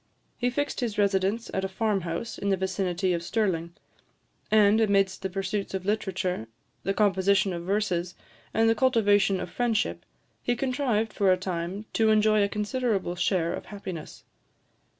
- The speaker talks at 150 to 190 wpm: Yes, average, 160 wpm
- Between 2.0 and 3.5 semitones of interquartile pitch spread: Yes, narrow, 2.6 semitones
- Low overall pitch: No, high, 200 Hz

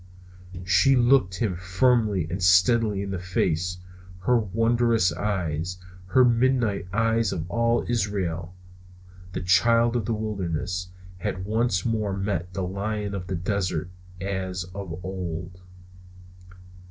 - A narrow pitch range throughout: No, average, 3.9 semitones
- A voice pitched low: Yes, very low, 95 Hz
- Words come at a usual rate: No, slow, 125 wpm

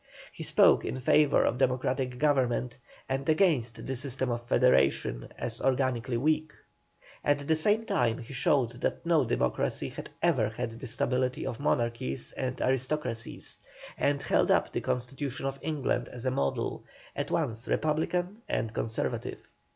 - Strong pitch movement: No, average, 3.3 semitones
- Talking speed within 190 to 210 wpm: No, average, 150 wpm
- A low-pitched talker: Yes, low, 130 Hz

